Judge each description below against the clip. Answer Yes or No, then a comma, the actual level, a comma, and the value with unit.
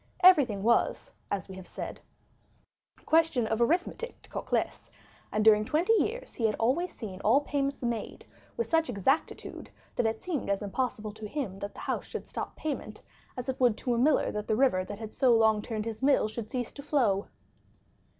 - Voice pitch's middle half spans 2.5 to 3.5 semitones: No, average, 4.9 semitones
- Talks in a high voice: Yes, high, 235 Hz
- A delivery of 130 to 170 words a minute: No, average, 195 wpm